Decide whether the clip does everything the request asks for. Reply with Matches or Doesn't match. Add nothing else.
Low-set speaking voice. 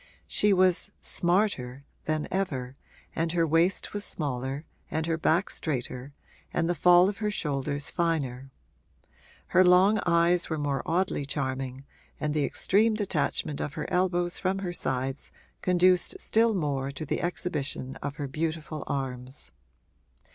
Doesn't match